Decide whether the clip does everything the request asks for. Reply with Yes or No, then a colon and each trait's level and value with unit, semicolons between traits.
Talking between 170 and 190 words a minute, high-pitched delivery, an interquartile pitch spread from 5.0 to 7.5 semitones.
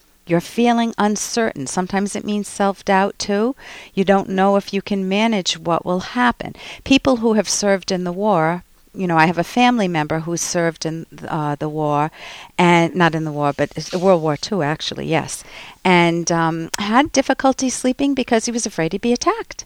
Yes: average, 185 wpm; high, 195 Hz; wide, 5.5 semitones